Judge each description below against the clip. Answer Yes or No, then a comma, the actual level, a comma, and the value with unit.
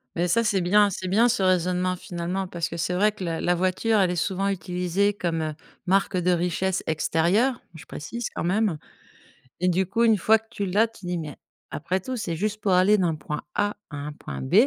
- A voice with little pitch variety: No, average, 3.2 semitones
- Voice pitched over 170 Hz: Yes, medium, 185 Hz